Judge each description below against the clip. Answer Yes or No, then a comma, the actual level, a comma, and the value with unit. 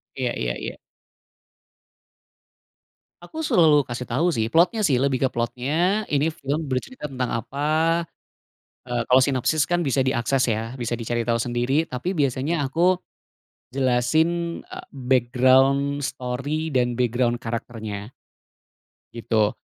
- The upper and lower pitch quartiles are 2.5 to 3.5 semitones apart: Yes, average, 3.2 semitones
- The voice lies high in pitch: No, low, 130 Hz